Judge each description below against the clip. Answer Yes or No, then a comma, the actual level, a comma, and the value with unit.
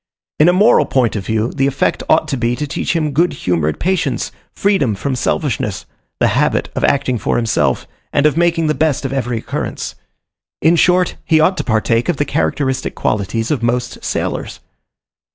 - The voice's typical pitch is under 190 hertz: Yes, low, 135 Hz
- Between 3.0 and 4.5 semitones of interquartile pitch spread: No, average, 5.3 semitones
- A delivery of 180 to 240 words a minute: Yes, average, 185 wpm